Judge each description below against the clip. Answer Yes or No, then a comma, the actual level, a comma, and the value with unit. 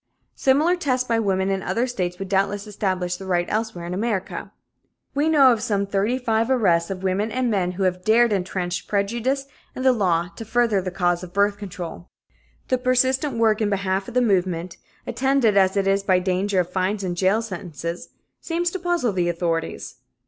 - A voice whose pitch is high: Yes, high, 200 Hz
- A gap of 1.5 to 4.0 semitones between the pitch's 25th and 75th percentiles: No, average, 4.4 semitones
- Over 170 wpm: Yes, average, 190 wpm